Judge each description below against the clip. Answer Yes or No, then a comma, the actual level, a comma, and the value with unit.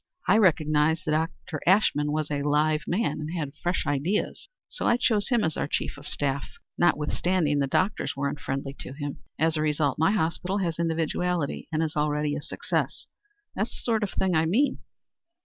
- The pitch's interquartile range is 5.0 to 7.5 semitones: No, average, 3.3 semitones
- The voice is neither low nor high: Yes, medium, 155 Hz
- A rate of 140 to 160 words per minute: No, average, 185 wpm